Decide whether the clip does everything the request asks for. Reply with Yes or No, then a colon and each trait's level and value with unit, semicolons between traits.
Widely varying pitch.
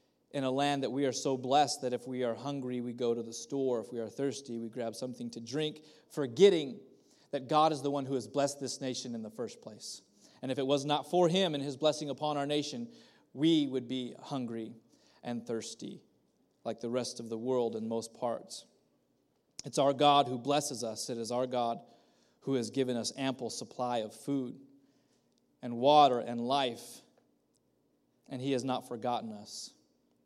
No: average, 3.1 semitones